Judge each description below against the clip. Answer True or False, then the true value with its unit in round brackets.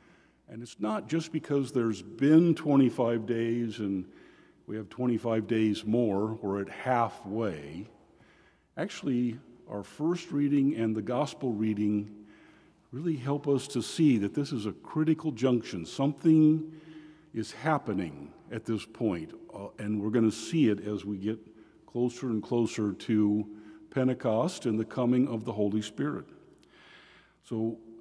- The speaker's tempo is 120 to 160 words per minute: True (140 wpm)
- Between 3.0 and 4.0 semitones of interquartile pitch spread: False (4.6 semitones)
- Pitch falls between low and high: False (115 Hz)